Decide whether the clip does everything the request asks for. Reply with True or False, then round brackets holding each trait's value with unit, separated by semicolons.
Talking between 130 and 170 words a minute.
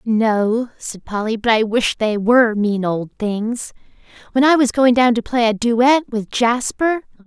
False (180 wpm)